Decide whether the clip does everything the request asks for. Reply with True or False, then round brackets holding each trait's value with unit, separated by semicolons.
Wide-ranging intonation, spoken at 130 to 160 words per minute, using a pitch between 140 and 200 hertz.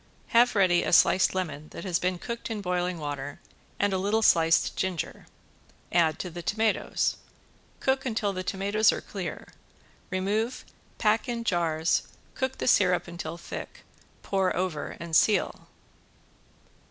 False (4.0 semitones; 140 wpm; 185 Hz)